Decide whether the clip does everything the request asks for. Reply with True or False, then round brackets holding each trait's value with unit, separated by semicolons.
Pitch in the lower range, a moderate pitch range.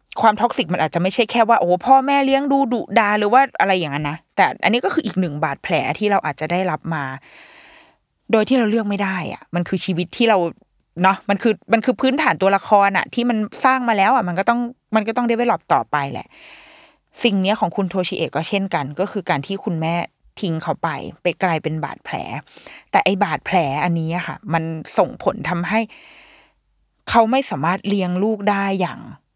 False (200 Hz; 5.0 semitones)